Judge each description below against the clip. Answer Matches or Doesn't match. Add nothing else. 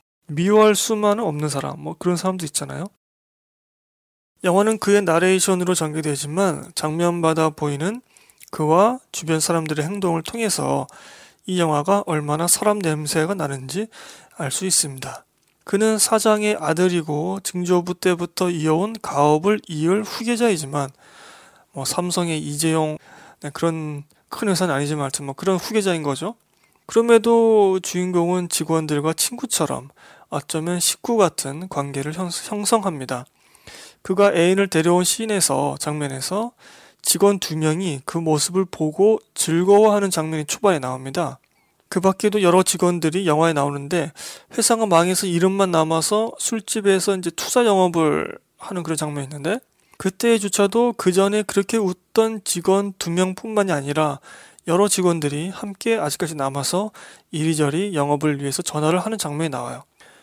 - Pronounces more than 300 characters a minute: Matches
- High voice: Doesn't match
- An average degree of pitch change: Matches